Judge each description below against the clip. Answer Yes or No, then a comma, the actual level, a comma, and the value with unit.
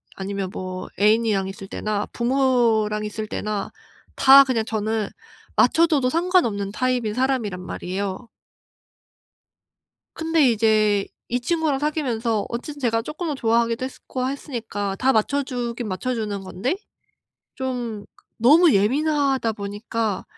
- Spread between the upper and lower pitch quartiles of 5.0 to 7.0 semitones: No, average, 4.2 semitones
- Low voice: No, high, 230 Hz